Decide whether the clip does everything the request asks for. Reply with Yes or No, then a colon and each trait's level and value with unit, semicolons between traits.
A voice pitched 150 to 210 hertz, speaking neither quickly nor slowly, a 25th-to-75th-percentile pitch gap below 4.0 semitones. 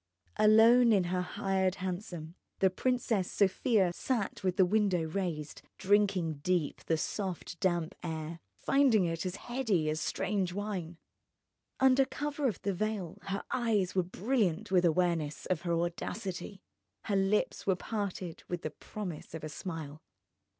Yes: medium, 185 Hz; average, 150 wpm; average, 3.5 semitones